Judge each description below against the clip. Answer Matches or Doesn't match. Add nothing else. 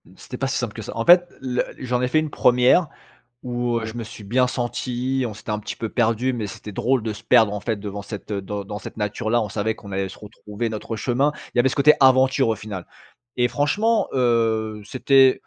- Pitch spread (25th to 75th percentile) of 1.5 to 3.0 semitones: Doesn't match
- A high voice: Doesn't match